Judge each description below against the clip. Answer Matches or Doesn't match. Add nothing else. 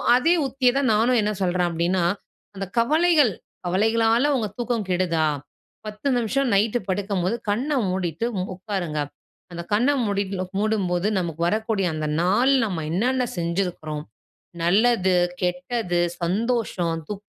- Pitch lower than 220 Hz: Matches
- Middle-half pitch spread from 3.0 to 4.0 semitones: Doesn't match